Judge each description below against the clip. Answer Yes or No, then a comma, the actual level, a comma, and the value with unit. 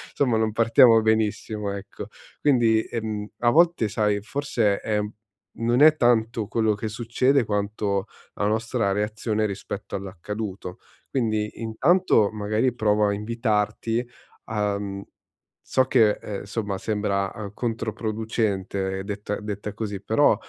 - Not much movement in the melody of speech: Yes, narrow, 2.0 semitones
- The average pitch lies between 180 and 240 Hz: No, low, 110 Hz